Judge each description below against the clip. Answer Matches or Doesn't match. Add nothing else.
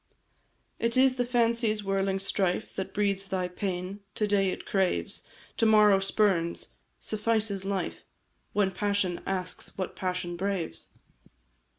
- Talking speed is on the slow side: Matches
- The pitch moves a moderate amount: Doesn't match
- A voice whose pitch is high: Matches